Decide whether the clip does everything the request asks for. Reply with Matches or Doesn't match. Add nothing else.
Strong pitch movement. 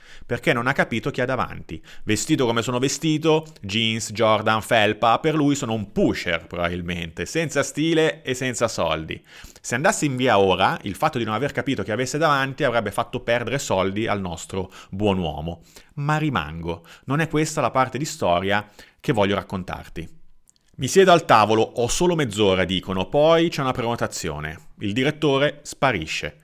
Matches